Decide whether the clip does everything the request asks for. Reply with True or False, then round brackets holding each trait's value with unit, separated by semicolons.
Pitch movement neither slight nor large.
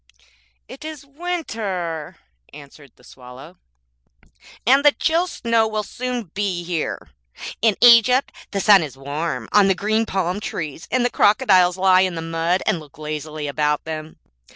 False (6.6 semitones)